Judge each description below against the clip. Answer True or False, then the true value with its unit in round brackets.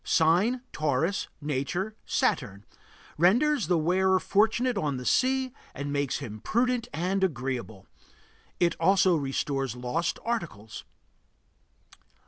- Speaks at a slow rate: True (110 wpm)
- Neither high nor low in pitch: True (170 Hz)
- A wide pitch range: True (7.2 semitones)